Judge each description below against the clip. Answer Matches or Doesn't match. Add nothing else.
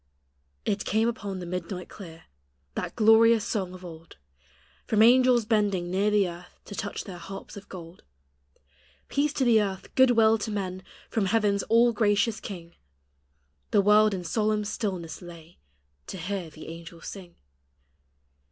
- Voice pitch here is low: Doesn't match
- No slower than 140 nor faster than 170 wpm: Matches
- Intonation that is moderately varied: Matches